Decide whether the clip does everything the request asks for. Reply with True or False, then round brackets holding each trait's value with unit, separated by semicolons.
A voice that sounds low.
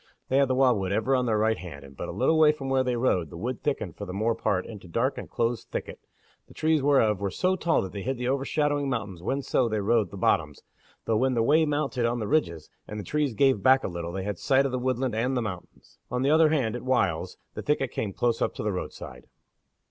True (120 Hz)